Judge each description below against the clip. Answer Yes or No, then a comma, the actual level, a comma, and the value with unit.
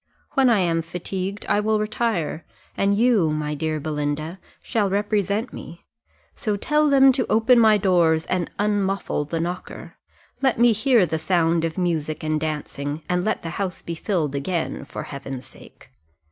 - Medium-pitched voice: Yes, medium, 180 Hz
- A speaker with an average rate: Yes, average, 165 wpm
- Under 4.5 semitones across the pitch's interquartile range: No, average, 5.1 semitones